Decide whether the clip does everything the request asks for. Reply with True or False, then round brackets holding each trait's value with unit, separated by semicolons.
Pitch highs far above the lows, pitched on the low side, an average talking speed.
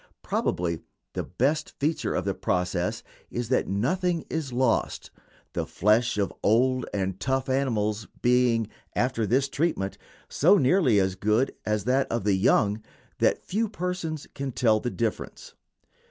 False (5.0 semitones; 120 Hz; 145 wpm)